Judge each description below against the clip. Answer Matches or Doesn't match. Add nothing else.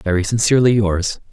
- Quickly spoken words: Doesn't match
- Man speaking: Matches